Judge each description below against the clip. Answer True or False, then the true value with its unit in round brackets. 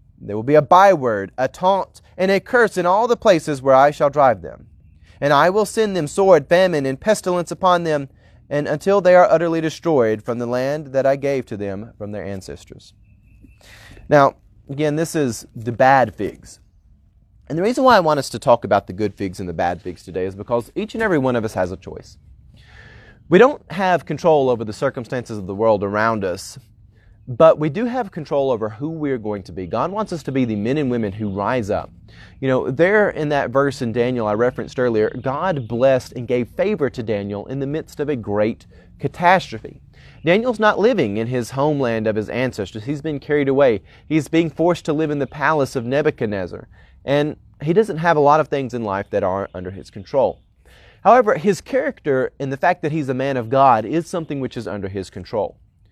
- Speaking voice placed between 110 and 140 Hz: True (135 Hz)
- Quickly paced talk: True (215 wpm)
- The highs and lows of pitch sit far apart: True (6.7 semitones)